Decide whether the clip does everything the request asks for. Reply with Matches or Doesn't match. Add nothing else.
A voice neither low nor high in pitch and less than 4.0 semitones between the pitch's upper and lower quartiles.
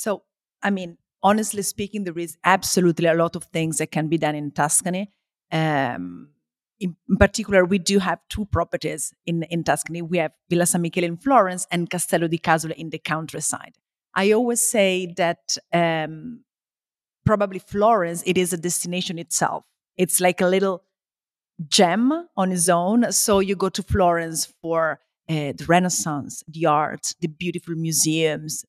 Matches